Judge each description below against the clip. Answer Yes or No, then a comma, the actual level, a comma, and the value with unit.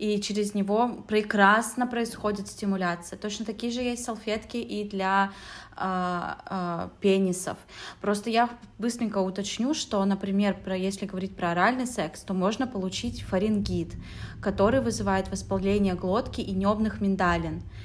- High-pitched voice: Yes, high, 200 Hz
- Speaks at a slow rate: No, average, 130 wpm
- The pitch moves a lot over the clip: No, narrow, 2.5 semitones